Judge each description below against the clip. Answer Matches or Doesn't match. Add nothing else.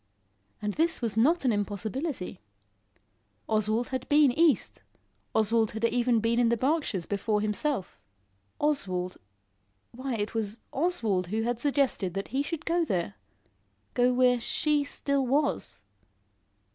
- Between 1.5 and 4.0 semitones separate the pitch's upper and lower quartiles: Doesn't match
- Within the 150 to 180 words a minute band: Doesn't match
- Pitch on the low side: Doesn't match